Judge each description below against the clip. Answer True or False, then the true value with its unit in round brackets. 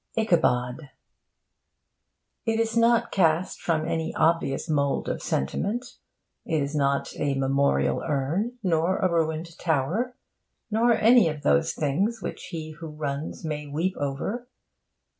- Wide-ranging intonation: True (5.7 semitones)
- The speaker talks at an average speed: False (130 wpm)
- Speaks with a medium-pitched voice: True (160 Hz)